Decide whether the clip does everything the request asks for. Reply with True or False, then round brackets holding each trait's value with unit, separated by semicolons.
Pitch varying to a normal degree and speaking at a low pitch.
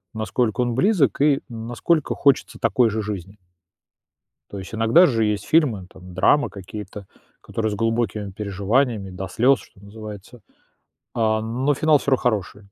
True (3.9 semitones; 110 Hz)